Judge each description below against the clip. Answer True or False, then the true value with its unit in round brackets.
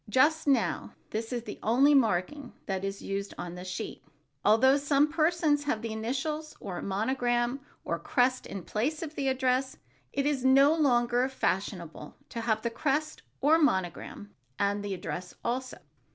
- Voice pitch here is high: True (250 Hz)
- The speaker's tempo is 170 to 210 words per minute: False (160 wpm)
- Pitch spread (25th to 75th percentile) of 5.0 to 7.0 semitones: True (5.5 semitones)